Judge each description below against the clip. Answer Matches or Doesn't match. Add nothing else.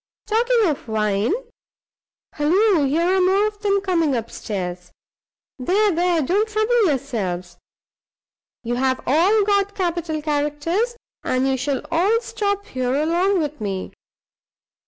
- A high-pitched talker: Matches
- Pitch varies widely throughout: Matches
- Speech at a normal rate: Doesn't match